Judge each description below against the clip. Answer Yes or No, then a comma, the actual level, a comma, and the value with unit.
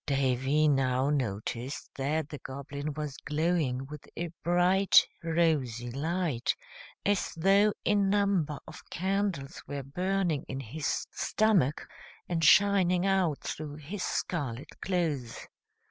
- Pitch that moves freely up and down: No, average, 4.9 semitones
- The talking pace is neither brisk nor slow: No, slow, 115 wpm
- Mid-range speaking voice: Yes, medium, 155 Hz